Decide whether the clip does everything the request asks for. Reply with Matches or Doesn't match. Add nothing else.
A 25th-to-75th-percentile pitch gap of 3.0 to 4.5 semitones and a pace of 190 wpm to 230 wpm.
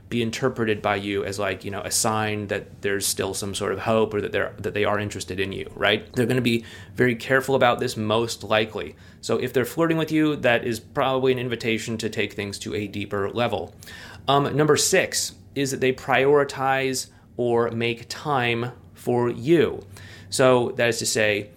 Matches